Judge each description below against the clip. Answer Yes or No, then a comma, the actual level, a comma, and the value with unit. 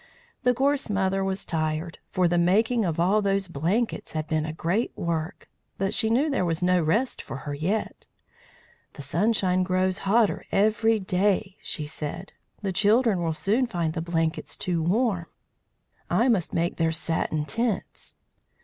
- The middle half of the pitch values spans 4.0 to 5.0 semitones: Yes, average, 4.6 semitones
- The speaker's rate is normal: Yes, average, 160 wpm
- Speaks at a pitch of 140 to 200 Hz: Yes, medium, 185 Hz